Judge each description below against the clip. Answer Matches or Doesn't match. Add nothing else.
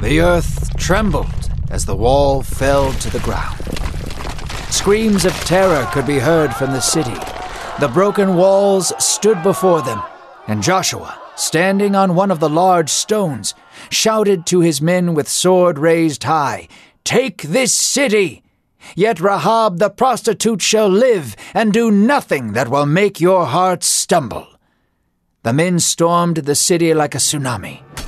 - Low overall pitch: Doesn't match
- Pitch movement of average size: Doesn't match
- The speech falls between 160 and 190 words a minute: Doesn't match